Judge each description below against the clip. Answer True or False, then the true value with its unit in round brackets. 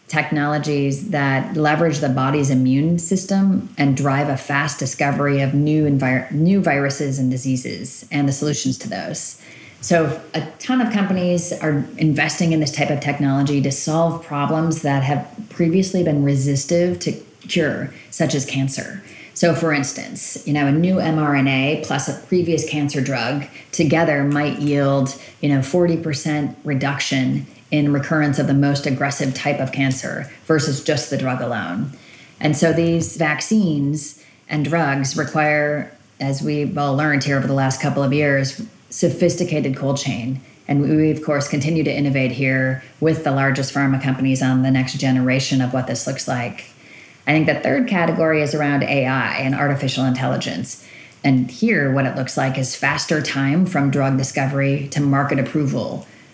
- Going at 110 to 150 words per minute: False (160 wpm)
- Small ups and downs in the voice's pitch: True (2.3 semitones)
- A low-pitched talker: False (145 Hz)